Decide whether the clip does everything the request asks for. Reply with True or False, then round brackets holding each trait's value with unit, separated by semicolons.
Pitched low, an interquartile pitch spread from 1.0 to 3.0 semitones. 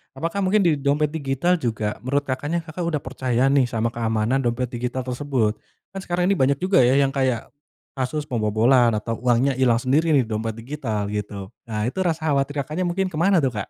False (130 Hz; 4.7 semitones)